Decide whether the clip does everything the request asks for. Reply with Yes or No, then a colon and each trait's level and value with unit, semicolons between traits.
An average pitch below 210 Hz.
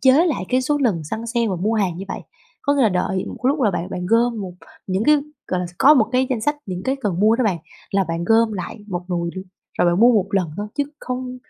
No: high, 215 Hz